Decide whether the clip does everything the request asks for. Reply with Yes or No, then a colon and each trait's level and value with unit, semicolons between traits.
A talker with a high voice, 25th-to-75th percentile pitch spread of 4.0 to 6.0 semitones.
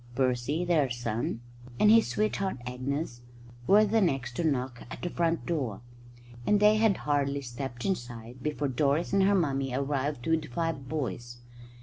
No: medium, 140 Hz; wide, 5.5 semitones